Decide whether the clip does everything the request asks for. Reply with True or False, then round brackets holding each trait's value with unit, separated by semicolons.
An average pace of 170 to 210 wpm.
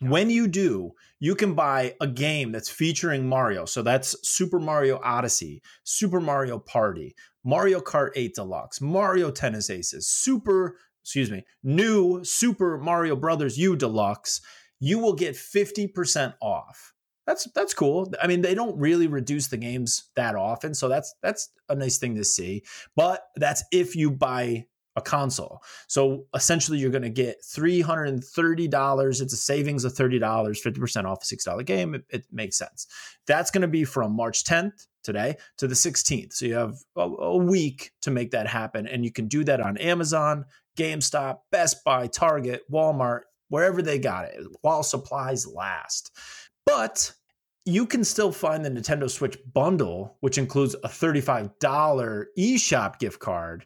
False (160 wpm)